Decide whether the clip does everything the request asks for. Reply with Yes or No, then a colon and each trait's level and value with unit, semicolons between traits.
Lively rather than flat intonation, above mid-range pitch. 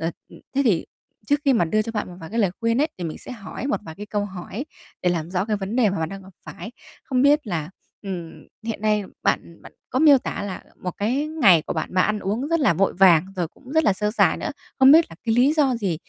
Yes: wide, 5.9 semitones; high, 210 Hz